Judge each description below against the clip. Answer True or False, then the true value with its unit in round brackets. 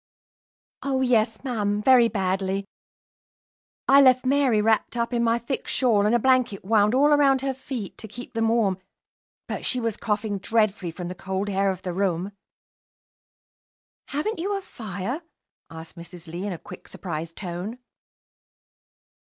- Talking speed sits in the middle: True (155 wpm)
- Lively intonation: False (4.9 semitones)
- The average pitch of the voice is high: True (220 Hz)